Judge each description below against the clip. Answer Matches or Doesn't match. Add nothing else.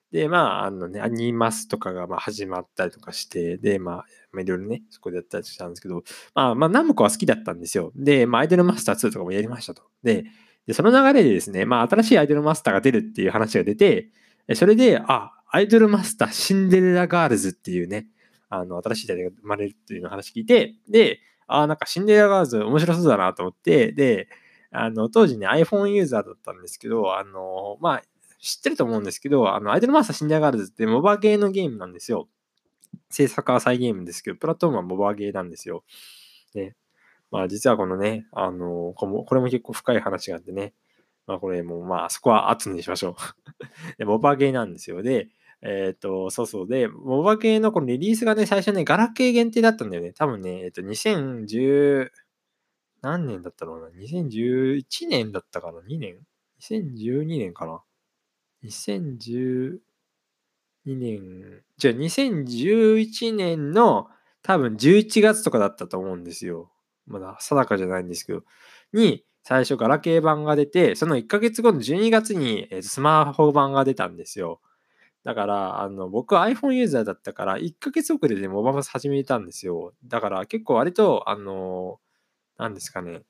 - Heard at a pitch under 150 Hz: Matches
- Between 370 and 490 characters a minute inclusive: Matches